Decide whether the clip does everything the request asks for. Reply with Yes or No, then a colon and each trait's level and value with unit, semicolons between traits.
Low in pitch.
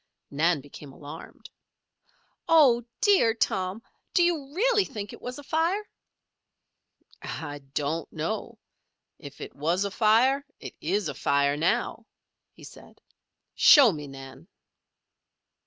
No: high, 205 Hz